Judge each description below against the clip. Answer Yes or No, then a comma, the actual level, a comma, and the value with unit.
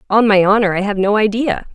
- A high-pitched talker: Yes, high, 205 Hz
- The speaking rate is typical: No, fast, 240 wpm